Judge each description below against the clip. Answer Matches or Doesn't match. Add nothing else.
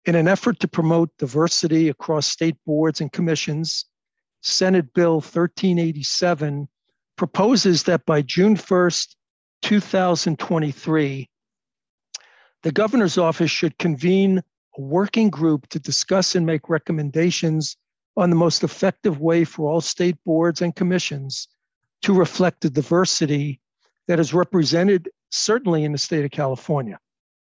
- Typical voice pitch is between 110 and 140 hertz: Doesn't match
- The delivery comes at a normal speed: Doesn't match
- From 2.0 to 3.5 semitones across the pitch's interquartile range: Matches